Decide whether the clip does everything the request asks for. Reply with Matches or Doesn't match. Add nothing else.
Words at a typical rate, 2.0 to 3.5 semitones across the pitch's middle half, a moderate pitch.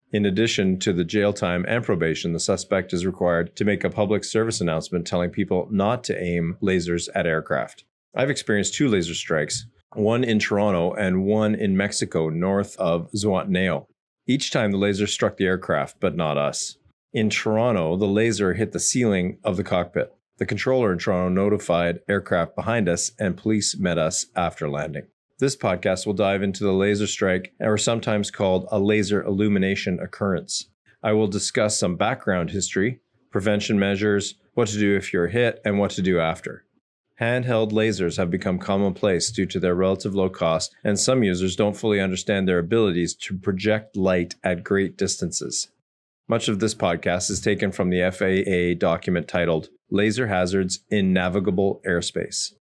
Doesn't match